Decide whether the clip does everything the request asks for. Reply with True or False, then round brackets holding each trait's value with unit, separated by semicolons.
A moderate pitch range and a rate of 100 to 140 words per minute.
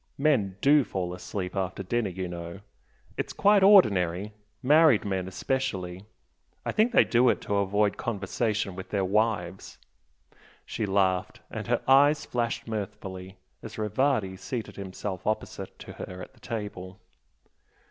True (4.2 semitones; 135 wpm)